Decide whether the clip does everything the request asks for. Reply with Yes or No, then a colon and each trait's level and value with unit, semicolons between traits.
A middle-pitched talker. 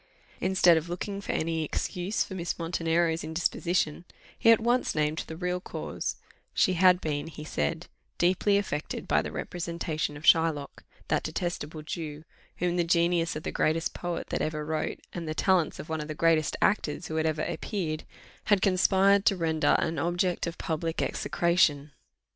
Yes: medium, 165 Hz